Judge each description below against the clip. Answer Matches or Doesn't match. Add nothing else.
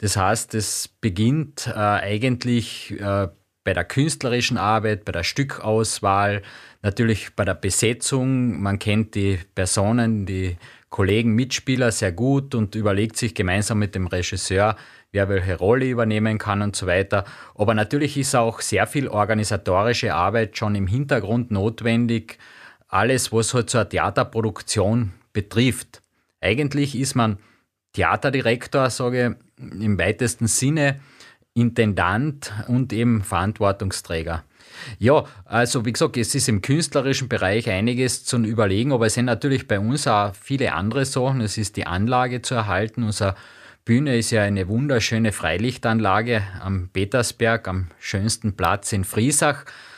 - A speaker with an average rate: Matches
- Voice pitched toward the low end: Matches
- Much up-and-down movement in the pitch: Doesn't match